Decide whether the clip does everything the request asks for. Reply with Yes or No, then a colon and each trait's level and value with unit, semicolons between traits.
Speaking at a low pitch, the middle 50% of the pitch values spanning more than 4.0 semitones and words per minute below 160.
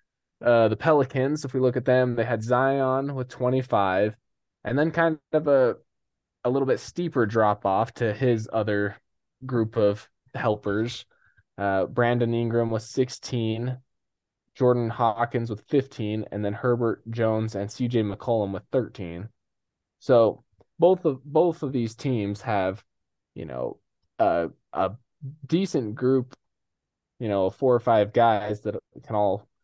No: low, 115 Hz; average, 3.7 semitones; average, 150 wpm